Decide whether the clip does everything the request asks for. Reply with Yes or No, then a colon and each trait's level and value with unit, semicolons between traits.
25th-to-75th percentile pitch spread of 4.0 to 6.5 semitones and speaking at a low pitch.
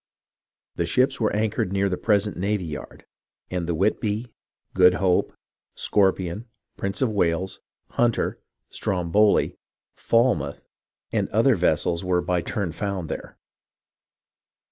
No: average, 3.2 semitones; very low, 95 Hz